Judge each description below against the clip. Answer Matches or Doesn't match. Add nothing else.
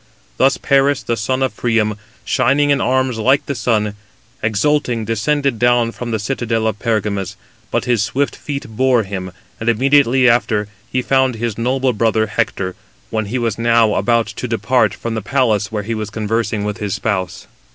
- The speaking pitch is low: Matches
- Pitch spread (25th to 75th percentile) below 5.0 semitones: Matches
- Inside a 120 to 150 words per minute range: Doesn't match